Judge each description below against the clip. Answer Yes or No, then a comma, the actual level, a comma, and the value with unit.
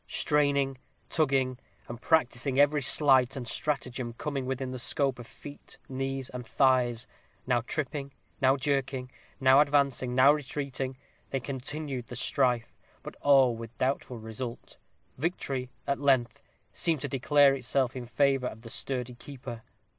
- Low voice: Yes, low, 130 Hz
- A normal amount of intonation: No, narrow, 2.0 semitones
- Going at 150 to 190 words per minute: No, average, 140 wpm